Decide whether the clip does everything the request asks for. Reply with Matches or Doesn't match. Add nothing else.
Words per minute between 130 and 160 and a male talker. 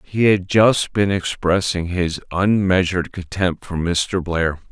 Matches